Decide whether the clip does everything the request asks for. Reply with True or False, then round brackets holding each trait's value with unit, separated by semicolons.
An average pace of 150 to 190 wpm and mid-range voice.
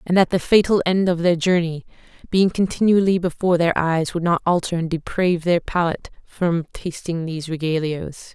True (170 wpm; 170 Hz)